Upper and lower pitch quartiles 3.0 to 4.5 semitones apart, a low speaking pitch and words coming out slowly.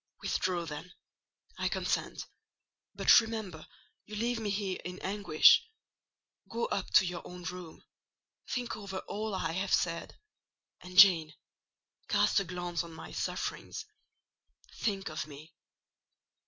No: average, 3.4 semitones; medium, 185 Hz; slow, 120 wpm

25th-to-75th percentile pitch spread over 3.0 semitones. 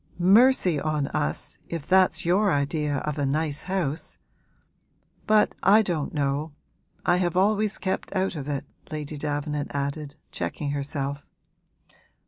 Yes: average, 4.5 semitones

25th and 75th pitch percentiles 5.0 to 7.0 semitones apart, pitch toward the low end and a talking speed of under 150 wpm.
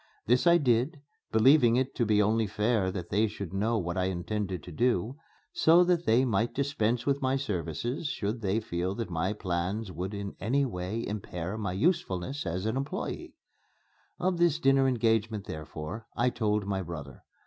No: wide, 5.4 semitones; low, 110 Hz; average, 175 wpm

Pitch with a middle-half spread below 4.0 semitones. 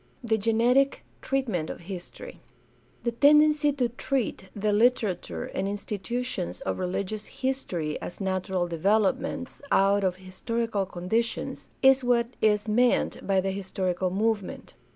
No: average, 4.3 semitones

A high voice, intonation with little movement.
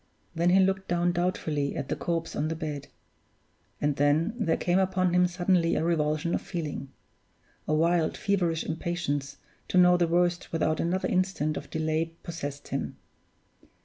No: medium, 170 Hz; narrow, 2.3 semitones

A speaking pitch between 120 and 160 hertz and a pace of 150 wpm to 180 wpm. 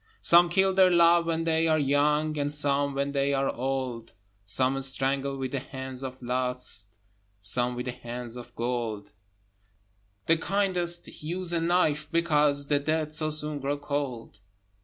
Yes: medium, 140 Hz; average, 160 wpm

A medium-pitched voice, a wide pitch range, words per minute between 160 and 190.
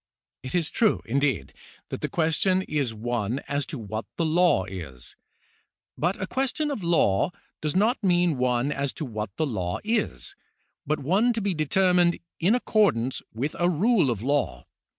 Yes: medium, 150 Hz; wide, 7.4 semitones; average, 170 wpm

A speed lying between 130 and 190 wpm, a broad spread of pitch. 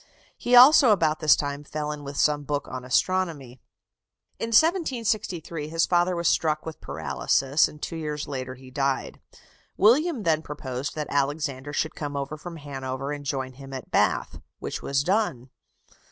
No: average, 165 wpm; average, 3.8 semitones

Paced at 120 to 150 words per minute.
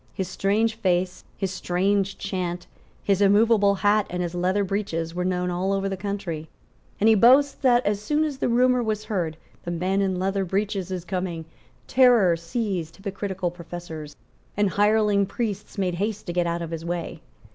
No: average, 180 wpm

